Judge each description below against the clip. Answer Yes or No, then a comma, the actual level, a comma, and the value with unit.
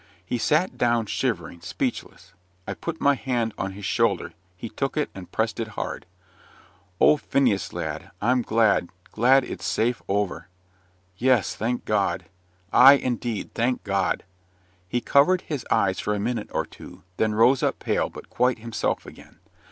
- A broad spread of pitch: No, average, 3.6 semitones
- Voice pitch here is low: Yes, low, 115 Hz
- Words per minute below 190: Yes, average, 160 wpm